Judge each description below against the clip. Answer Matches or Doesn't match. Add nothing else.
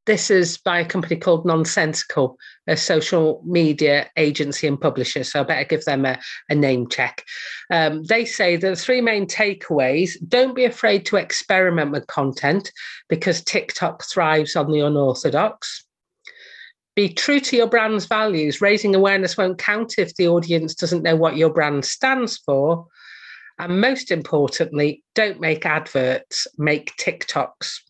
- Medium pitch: Matches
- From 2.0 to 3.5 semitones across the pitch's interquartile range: Doesn't match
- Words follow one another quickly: Doesn't match